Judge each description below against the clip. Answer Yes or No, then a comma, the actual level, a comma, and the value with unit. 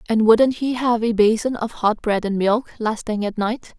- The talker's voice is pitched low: No, high, 225 Hz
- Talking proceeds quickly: Yes, fast, 240 wpm